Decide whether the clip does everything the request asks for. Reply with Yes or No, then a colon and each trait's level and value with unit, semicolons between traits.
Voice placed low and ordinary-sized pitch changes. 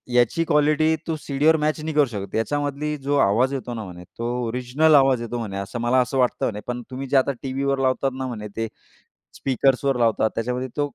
Yes: low, 130 Hz; average, 3.4 semitones